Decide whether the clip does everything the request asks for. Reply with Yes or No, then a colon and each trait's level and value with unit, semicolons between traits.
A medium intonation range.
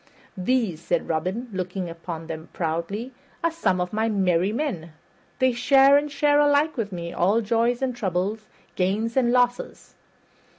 No: wide, 6.0 semitones